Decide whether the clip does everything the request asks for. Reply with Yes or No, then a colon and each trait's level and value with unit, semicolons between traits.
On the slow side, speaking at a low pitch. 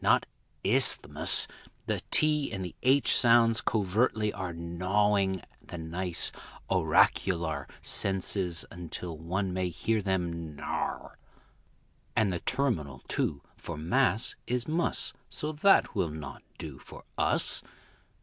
Yes: slow, 120 wpm; very low, 95 Hz